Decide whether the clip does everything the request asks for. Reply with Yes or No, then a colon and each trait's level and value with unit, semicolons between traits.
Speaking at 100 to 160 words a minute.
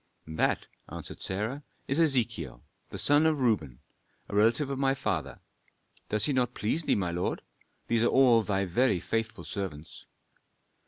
Yes: average, 155 wpm